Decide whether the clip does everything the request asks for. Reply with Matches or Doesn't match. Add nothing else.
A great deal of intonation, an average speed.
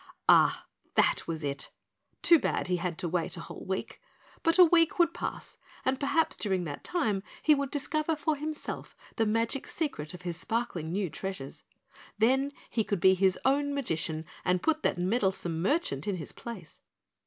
Matches